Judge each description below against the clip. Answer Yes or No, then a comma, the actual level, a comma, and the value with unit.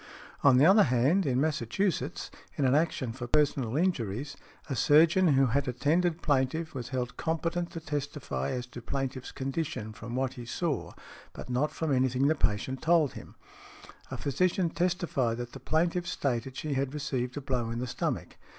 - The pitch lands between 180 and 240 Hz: No, medium, 140 Hz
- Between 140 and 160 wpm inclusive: No, average, 180 wpm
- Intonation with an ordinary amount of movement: Yes, average, 4.1 semitones